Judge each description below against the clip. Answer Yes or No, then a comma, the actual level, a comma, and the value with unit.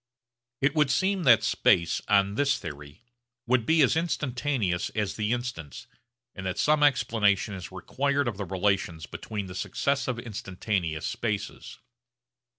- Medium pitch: No, low, 110 Hz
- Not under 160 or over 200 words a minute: No, average, 140 wpm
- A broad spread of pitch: Yes, wide, 6.2 semitones